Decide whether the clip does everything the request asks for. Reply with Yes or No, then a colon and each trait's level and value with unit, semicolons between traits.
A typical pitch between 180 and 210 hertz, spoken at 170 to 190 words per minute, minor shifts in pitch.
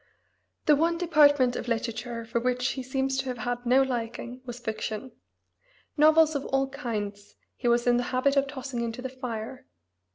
No: very high, 250 Hz; average, 175 wpm; narrow, 2.3 semitones